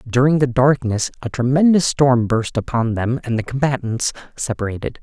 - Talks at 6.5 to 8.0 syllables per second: No, 5.0 syllables/s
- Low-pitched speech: Yes, low, 125 Hz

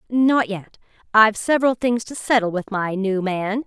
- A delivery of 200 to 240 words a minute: No, average, 180 wpm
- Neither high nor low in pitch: No, high, 215 Hz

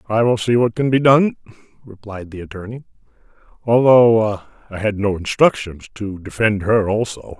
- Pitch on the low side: Yes, low, 110 Hz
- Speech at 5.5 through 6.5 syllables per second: No, 4.9 syllables/s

